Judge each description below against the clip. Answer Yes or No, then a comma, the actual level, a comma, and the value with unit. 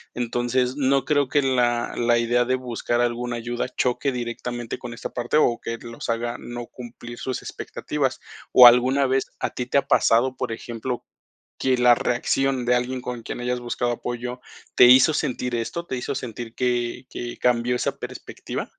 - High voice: No, low, 125 Hz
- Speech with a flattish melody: Yes, narrow, 1.3 semitones